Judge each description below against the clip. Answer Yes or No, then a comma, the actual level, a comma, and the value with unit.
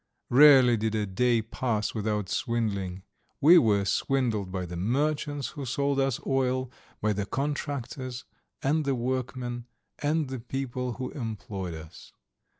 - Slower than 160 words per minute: Yes, average, 140 wpm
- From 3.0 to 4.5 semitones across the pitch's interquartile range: Yes, average, 4.2 semitones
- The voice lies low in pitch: Yes, low, 125 Hz